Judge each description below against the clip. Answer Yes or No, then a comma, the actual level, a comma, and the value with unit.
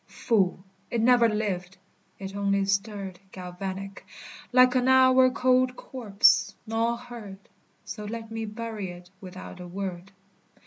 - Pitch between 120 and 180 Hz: No, high, 210 Hz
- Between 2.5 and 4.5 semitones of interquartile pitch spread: Yes, average, 3.6 semitones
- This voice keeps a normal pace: No, slow, 130 wpm